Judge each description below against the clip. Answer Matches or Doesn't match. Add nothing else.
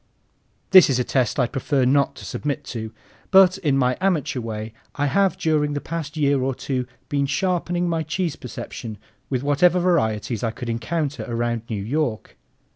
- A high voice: Doesn't match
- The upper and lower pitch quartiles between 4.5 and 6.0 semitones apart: Matches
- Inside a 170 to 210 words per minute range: Matches